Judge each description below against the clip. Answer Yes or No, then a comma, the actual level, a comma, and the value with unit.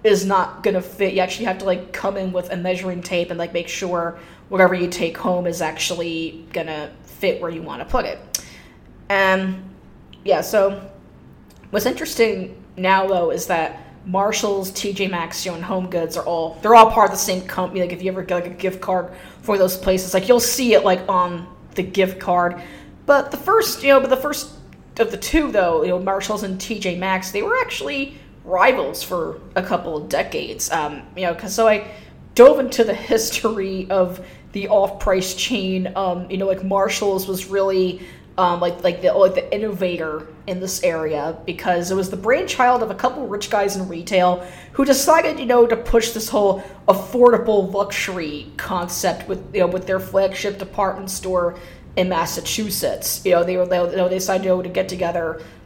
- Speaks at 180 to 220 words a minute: Yes, average, 200 wpm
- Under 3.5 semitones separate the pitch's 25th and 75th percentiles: Yes, narrow, 2.5 semitones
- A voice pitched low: No, high, 190 Hz